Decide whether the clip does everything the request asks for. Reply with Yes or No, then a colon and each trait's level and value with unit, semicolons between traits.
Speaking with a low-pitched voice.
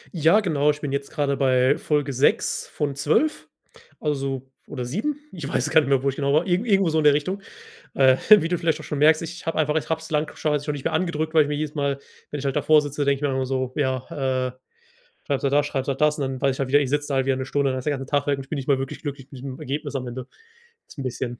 No: medium, 145 Hz